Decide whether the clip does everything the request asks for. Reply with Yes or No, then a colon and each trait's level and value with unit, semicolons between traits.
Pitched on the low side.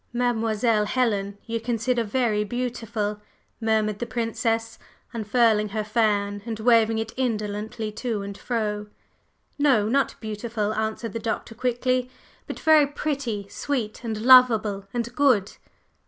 No: high, 225 Hz